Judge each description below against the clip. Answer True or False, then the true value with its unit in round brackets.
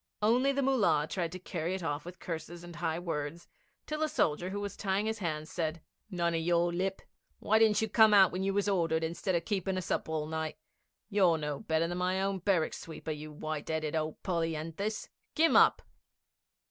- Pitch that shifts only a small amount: False (3.7 semitones)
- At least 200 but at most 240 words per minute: True (205 wpm)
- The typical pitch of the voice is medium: True (175 Hz)